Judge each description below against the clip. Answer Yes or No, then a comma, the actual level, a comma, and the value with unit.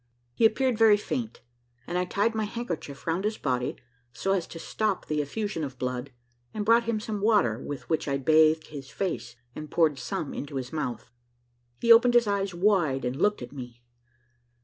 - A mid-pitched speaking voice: Yes, medium, 175 Hz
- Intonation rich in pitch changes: Yes, wide, 7.3 semitones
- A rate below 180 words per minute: No, average, 190 wpm